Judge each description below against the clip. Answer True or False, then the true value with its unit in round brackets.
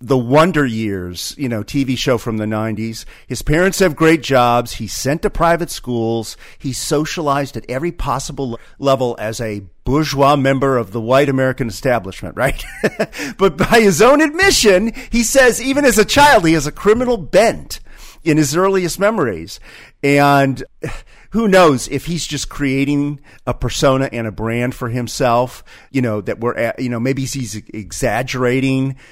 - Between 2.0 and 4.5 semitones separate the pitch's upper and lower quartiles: False (5.1 semitones)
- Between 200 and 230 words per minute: False (165 wpm)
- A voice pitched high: False (135 Hz)